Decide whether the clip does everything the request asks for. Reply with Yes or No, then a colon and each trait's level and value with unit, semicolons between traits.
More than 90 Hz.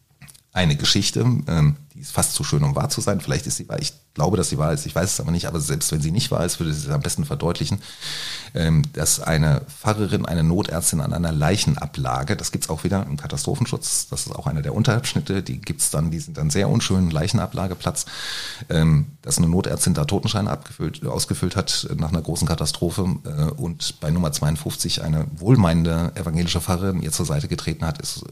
No: very low, 85 Hz